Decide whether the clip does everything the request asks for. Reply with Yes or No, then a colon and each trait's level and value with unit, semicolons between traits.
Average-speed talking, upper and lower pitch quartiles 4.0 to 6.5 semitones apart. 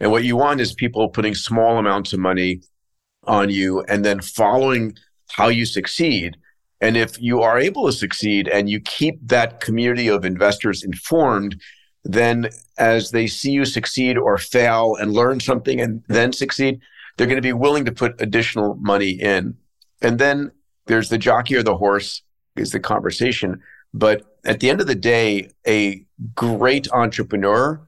No: average, 170 wpm; average, 3.1 semitones